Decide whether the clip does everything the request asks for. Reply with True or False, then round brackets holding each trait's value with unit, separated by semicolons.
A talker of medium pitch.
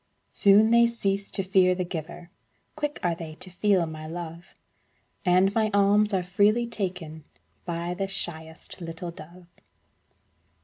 True (180 Hz)